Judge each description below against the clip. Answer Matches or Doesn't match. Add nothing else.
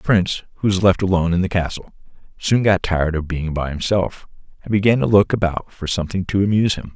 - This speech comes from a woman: Doesn't match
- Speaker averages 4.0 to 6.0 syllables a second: Doesn't match